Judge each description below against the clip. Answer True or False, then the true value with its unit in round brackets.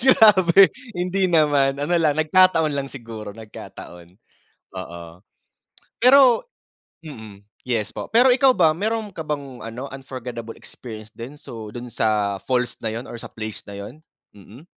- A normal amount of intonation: False (7.6 semitones)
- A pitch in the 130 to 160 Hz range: True (135 Hz)